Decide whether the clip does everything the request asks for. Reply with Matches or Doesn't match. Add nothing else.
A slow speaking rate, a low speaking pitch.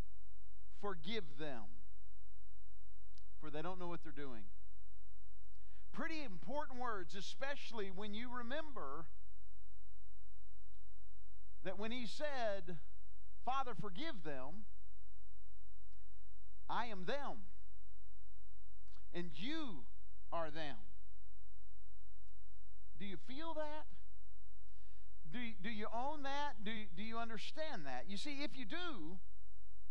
Matches